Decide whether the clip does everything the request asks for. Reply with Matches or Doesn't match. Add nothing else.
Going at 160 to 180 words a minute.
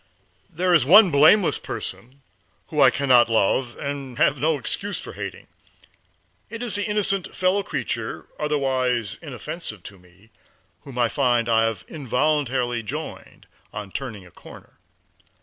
Doesn't match